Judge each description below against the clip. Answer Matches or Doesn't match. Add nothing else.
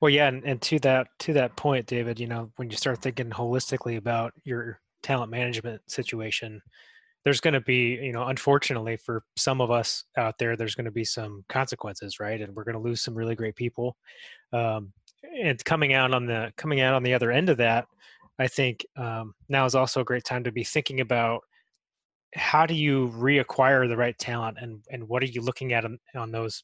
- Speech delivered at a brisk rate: Matches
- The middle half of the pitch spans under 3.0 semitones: Matches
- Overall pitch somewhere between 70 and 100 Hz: Doesn't match